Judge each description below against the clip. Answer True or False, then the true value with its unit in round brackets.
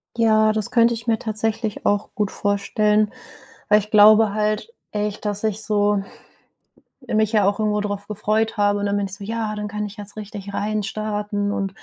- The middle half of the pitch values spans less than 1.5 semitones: True (1.0 semitones)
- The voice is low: False (210 Hz)